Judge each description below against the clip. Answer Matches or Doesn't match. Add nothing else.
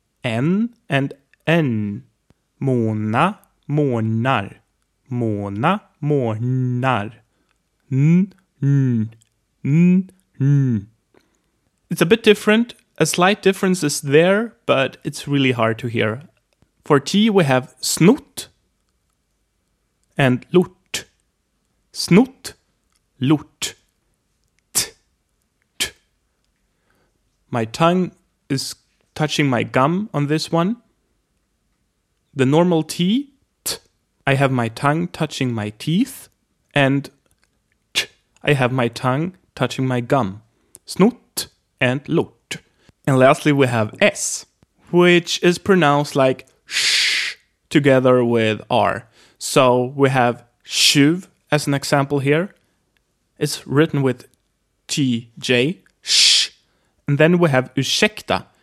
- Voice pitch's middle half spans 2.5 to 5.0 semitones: Doesn't match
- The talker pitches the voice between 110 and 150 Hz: Matches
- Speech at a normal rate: Doesn't match